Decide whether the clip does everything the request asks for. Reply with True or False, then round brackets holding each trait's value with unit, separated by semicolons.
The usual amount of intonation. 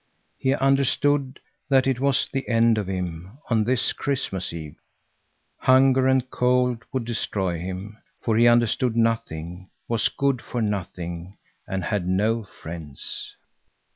False (5.8 semitones)